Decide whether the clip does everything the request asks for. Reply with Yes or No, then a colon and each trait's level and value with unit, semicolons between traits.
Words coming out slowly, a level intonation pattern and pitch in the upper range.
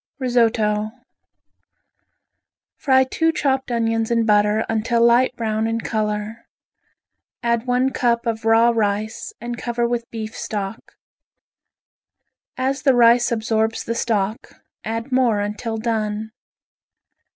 Yes: slow, 115 wpm; narrow, 1.7 semitones; high, 230 Hz